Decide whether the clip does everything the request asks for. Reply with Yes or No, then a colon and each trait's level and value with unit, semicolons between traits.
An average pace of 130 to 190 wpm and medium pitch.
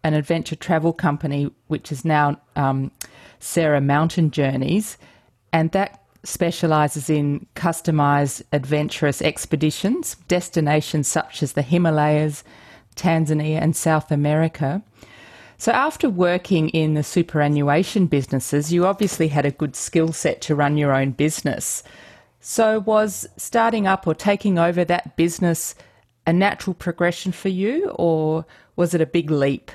Yes: slow, 135 wpm; medium, 160 Hz